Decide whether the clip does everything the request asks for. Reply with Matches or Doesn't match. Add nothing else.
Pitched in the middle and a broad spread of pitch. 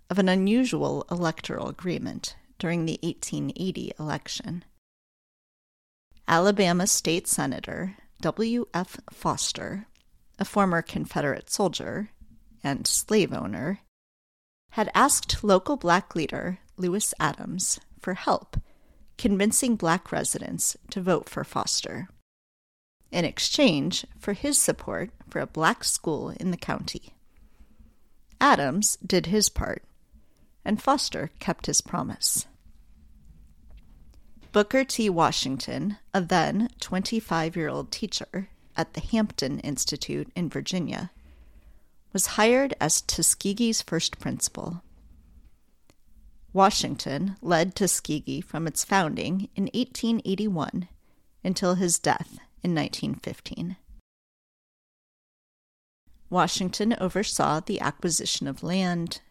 Matches